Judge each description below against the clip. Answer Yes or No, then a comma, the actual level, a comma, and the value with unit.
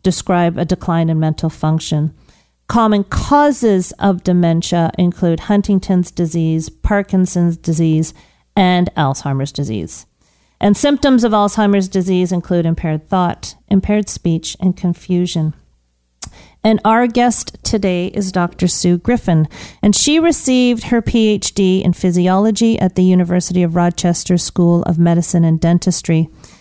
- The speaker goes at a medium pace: No, slow, 125 wpm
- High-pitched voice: No, medium, 180 Hz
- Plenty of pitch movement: No, average, 3.3 semitones